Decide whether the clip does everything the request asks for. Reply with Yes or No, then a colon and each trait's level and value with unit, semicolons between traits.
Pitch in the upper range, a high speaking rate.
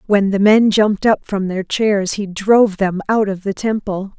Yes: high, 200 Hz; fast, 215 wpm